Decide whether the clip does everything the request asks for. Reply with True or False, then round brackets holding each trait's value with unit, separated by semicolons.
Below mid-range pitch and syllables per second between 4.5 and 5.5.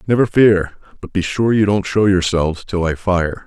True (95 Hz; 4.9 syllables/s)